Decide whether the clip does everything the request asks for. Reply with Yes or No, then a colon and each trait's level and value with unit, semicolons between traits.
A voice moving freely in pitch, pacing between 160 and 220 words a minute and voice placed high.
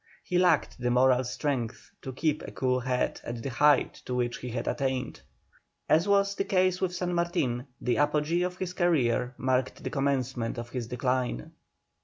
No: wide, 5.7 semitones; average, 180 wpm; low, 130 Hz